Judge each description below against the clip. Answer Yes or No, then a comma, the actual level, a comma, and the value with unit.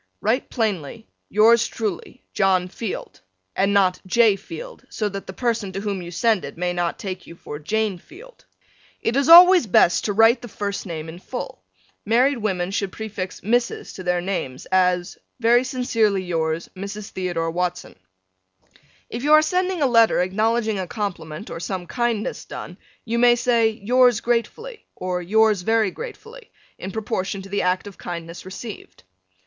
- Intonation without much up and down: No, average, 4.5 semitones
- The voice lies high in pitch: Yes, high, 205 Hz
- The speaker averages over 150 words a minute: Yes, average, 165 wpm